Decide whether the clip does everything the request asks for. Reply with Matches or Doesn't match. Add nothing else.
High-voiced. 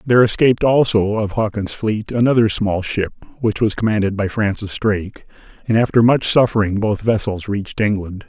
Doesn't match